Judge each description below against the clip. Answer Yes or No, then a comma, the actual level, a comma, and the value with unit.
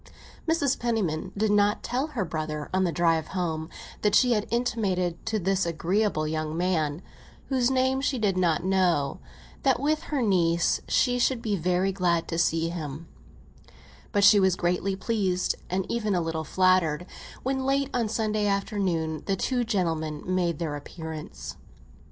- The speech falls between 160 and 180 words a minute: Yes, average, 165 wpm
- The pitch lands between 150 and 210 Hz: Yes, medium, 185 Hz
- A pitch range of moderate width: Yes, average, 5.0 semitones